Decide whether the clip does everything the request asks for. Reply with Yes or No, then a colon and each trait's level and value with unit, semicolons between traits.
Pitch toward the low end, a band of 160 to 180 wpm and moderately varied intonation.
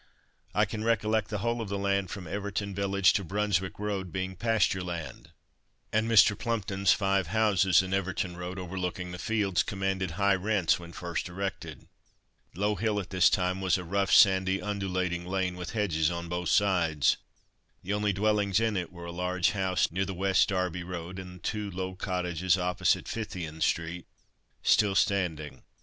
No: very low, 95 Hz; average, 170 wpm; narrow, 2.1 semitones